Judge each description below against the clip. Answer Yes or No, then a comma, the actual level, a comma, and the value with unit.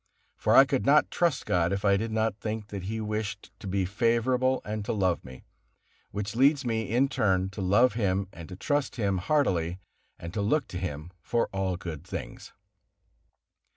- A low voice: Yes, low, 105 Hz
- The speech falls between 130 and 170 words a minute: No, average, 190 wpm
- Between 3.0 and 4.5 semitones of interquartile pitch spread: Yes, average, 4.1 semitones